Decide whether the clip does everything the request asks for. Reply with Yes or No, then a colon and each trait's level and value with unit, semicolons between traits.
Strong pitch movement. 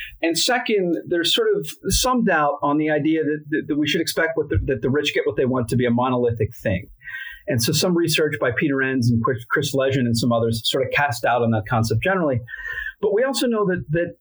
Yes: wide, 6.7 semitones